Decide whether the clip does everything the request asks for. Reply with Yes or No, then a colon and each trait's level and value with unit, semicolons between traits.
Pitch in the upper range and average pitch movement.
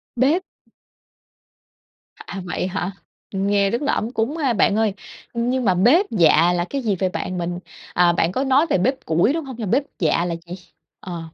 No: high, 200 Hz; wide, 6.5 semitones